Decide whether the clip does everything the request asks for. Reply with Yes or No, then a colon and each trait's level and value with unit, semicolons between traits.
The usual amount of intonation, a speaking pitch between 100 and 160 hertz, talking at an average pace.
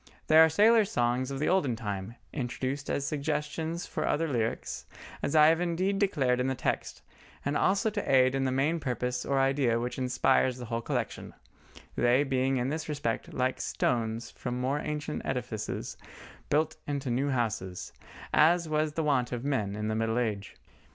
Yes: average, 3.9 semitones; low, 135 Hz; average, 175 wpm